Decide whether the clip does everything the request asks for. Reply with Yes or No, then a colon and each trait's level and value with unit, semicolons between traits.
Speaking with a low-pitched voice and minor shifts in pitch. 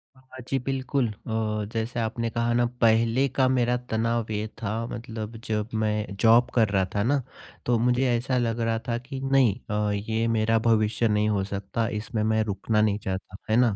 Yes: low, 115 Hz; narrow, 2.0 semitones